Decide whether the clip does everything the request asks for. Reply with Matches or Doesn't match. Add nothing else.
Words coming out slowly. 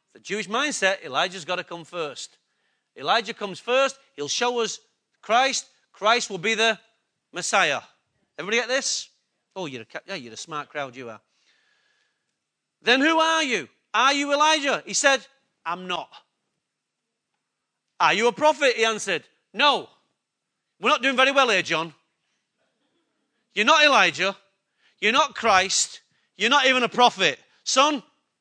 Doesn't match